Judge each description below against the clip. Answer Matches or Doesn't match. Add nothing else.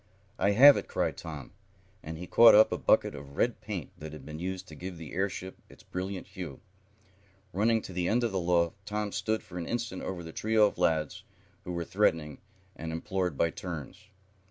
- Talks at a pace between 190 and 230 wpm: Matches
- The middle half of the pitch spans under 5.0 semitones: Matches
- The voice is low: Matches